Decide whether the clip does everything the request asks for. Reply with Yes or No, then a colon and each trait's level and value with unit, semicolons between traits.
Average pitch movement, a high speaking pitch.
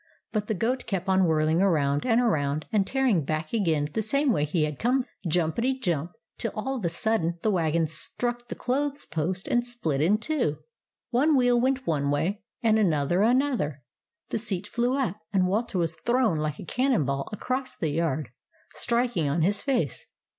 No: wide, 7.3 semitones; high, 195 Hz